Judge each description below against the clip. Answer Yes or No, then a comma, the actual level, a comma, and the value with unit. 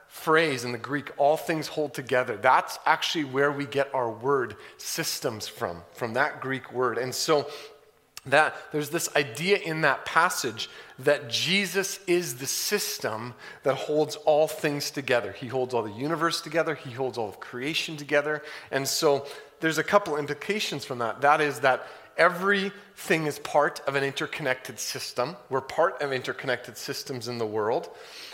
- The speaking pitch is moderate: Yes, medium, 145 Hz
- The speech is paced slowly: No, average, 165 wpm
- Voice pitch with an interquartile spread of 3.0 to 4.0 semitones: Yes, average, 3.3 semitones